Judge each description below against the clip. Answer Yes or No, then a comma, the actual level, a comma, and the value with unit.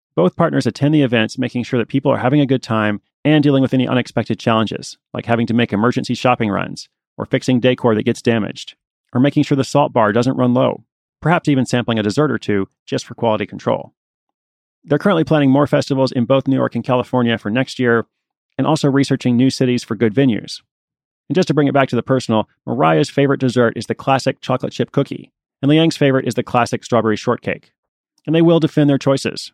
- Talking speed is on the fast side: Yes, fast, 215 wpm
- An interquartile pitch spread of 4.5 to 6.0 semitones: No, average, 3.1 semitones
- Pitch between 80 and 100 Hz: No, low, 130 Hz